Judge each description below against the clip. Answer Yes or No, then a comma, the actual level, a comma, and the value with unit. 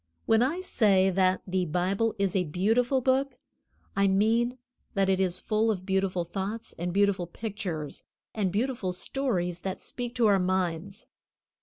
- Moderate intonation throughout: Yes, average, 3.6 semitones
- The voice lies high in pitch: Yes, high, 195 Hz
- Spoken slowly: No, average, 155 wpm